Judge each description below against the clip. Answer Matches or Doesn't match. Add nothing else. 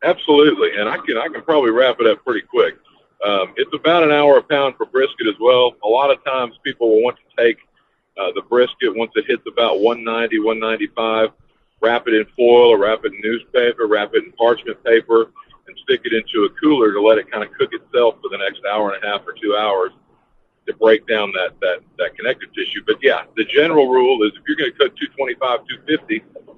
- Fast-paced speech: Matches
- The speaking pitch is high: Matches